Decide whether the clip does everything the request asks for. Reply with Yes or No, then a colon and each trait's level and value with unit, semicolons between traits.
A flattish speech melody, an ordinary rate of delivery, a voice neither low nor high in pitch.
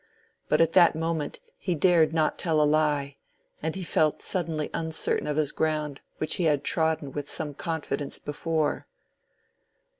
Yes: narrow, 1.7 semitones; average, 155 wpm; medium, 155 Hz